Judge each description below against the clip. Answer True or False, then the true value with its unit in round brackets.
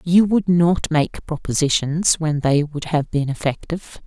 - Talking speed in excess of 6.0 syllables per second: False (4.3 syllables/s)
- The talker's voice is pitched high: False (160 Hz)